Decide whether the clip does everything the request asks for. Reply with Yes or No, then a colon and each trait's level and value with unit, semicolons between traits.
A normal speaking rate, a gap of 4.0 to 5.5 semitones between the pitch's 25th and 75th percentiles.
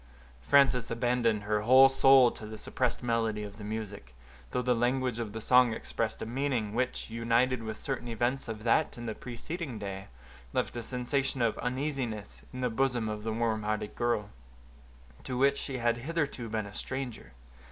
No: average, 180 wpm; average, 2.7 semitones